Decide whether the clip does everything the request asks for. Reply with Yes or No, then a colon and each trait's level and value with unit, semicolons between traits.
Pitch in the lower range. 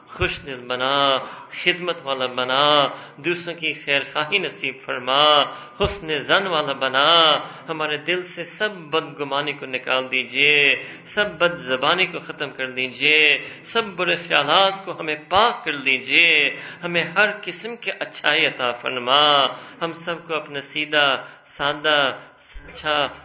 No: medium, 150 Hz